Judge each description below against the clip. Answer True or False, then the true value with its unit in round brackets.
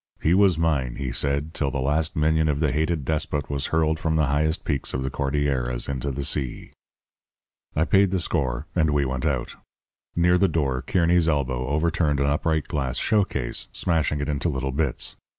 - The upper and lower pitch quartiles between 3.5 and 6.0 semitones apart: False (2.9 semitones)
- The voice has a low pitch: True (75 Hz)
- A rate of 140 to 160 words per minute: False (185 wpm)